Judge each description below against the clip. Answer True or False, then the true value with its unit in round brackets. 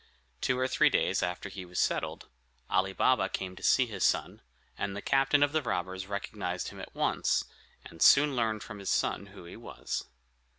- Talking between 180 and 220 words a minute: True (195 wpm)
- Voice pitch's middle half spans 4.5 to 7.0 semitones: True (5.5 semitones)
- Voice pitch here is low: True (100 Hz)